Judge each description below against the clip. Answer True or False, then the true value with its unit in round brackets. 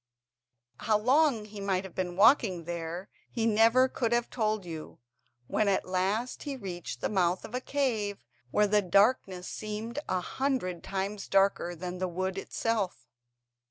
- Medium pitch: False (200 Hz)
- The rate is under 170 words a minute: True (160 wpm)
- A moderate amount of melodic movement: True (3.7 semitones)